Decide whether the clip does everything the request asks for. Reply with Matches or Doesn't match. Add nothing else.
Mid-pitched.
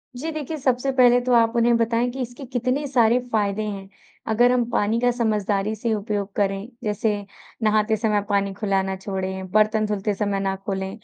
Doesn't match